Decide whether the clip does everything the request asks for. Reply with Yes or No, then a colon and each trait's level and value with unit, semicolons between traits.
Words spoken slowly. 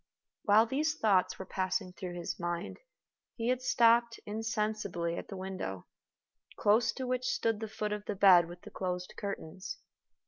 No: average, 165 wpm